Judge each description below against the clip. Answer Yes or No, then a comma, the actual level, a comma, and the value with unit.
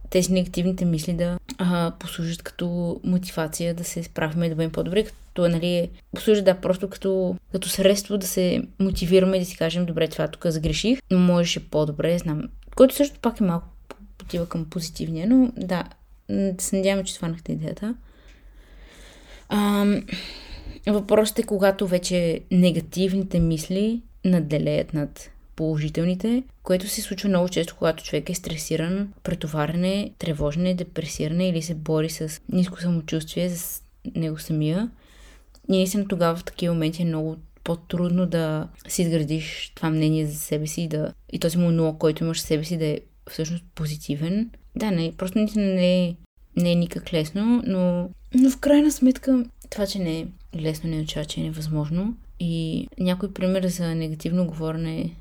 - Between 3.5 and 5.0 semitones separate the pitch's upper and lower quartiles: No, average, 3.0 semitones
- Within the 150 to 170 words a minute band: Yes, average, 160 wpm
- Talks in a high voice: No, medium, 175 Hz